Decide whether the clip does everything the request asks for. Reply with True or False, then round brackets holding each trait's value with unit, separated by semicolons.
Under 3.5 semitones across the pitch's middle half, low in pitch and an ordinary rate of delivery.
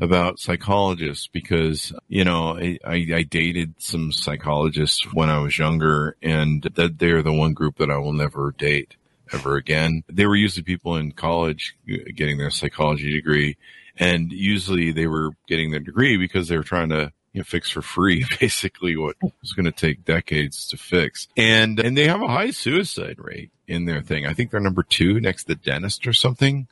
True (3.1 semitones; 80 Hz; 190 wpm)